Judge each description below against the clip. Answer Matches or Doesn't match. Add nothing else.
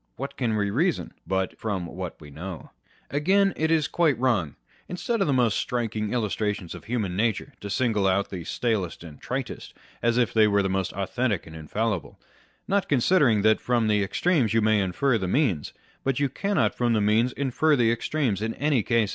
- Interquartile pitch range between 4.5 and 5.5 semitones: Matches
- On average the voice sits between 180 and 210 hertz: Doesn't match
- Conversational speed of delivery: Matches